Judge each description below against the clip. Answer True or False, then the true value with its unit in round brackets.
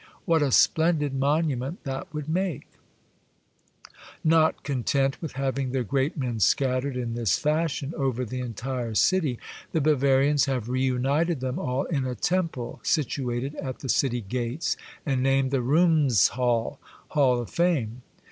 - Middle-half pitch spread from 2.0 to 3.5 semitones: True (3.2 semitones)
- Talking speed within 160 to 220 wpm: False (145 wpm)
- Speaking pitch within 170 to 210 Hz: False (135 Hz)